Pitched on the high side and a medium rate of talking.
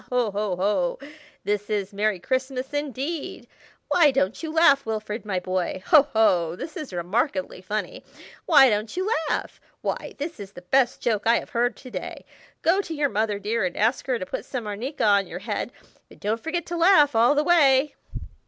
Yes: high, 230 Hz; average, 190 wpm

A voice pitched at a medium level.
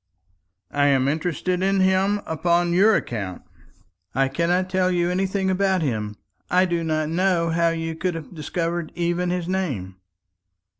Yes: medium, 175 Hz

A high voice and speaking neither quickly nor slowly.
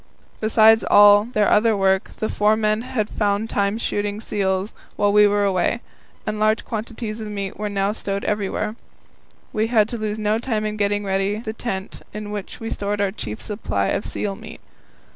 Yes: high, 210 Hz; average, 190 wpm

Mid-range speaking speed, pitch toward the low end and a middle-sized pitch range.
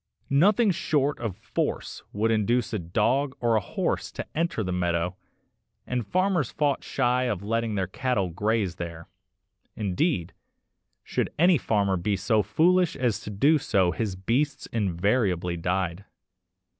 No: average, 145 wpm; low, 110 Hz; wide, 6.4 semitones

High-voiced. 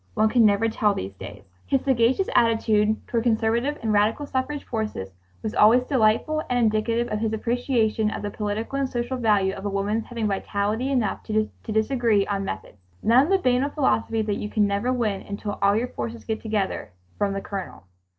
Yes: high, 220 Hz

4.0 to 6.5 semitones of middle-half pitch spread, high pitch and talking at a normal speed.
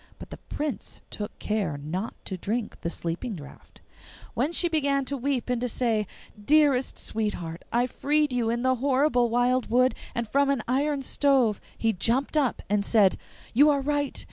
Yes: average, 4.4 semitones; very high, 250 Hz; average, 175 wpm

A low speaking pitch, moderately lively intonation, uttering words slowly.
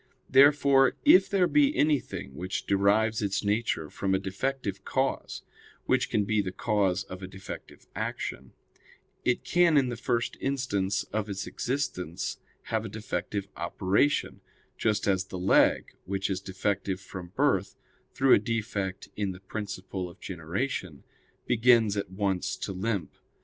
No: low, 100 Hz; average, 4.2 semitones; average, 145 wpm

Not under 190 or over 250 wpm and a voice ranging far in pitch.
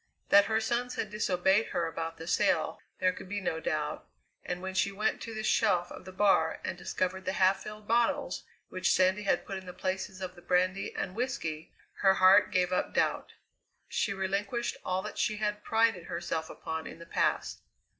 No: average, 195 wpm; narrow, 2.6 semitones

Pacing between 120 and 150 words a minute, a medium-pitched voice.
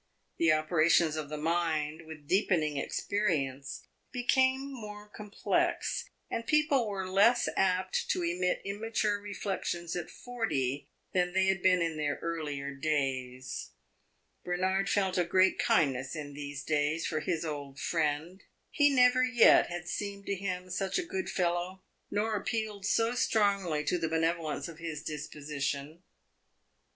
Yes: average, 140 wpm; medium, 175 Hz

